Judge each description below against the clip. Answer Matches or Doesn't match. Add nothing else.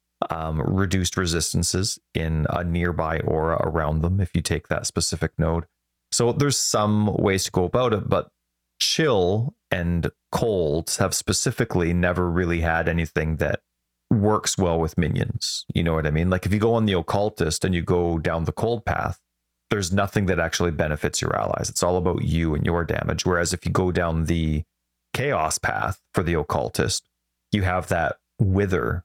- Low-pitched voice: Matches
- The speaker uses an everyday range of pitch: Matches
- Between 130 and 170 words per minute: Doesn't match